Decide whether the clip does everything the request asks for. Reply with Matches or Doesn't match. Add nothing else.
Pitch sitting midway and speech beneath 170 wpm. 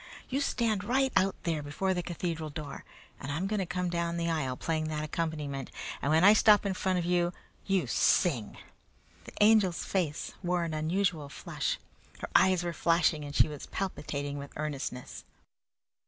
Doesn't match